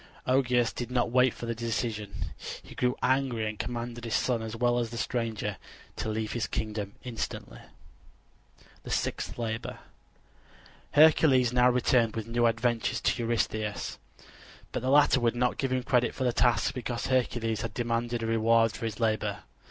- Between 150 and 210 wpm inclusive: Yes, average, 165 wpm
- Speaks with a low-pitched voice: Yes, low, 120 Hz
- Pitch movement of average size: No, narrow, 1.7 semitones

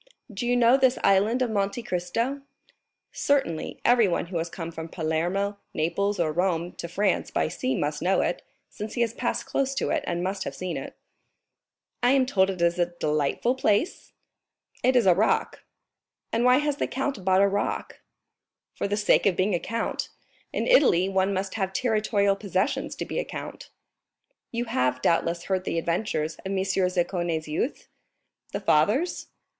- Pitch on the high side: Yes, high, 195 Hz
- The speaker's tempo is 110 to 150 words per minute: No, average, 175 wpm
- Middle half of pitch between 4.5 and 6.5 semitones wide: Yes, average, 5.0 semitones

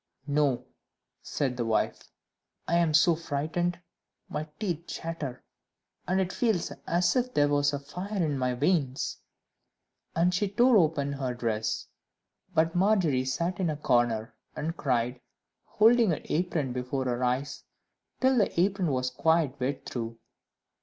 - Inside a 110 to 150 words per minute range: Yes, average, 145 wpm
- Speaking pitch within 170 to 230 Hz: No, medium, 150 Hz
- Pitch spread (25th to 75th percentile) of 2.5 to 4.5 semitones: No, wide, 5.5 semitones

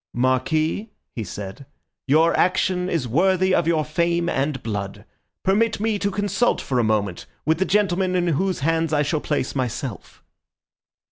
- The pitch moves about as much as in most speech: No, wide, 5.9 semitones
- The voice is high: No, medium, 165 Hz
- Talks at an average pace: Yes, average, 155 wpm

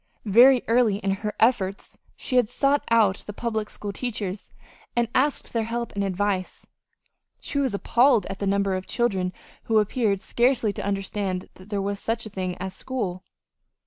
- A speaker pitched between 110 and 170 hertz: No, high, 210 Hz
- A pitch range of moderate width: Yes, average, 3.4 semitones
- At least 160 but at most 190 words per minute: Yes, average, 175 wpm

